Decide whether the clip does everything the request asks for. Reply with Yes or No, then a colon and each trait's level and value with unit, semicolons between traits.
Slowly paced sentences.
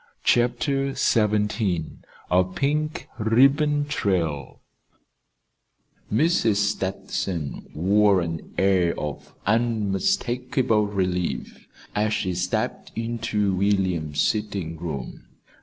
Yes: slow, 80 wpm